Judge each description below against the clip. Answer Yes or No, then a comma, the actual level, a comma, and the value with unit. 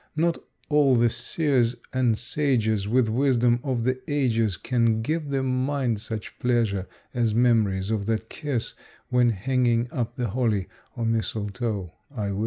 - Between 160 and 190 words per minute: No, average, 150 wpm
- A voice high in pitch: No, low, 120 Hz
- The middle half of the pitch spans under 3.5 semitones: Yes, average, 2.8 semitones